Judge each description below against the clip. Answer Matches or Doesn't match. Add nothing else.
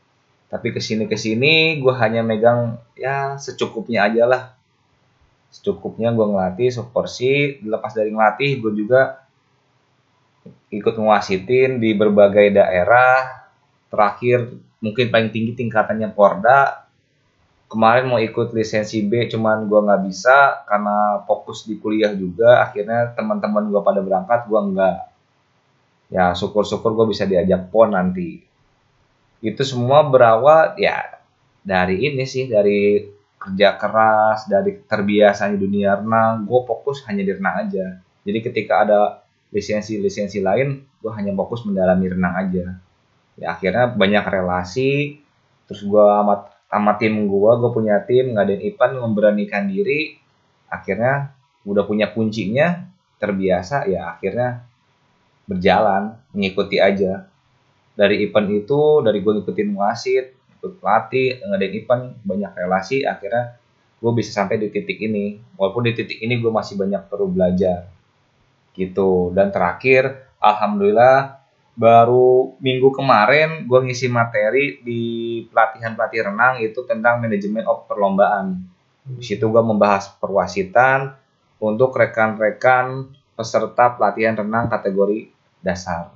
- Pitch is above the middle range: Doesn't match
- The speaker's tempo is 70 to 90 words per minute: Doesn't match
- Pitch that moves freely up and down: Doesn't match